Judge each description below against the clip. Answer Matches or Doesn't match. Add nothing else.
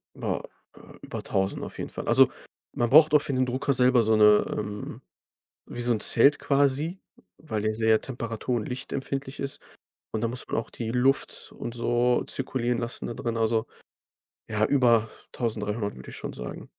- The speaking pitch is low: Matches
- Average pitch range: Matches